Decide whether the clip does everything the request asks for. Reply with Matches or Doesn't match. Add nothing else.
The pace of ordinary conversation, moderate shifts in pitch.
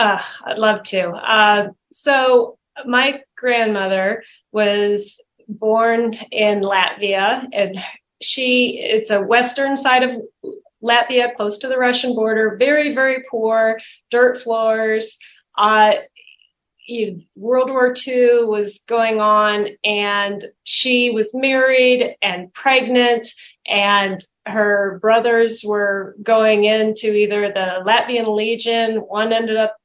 Doesn't match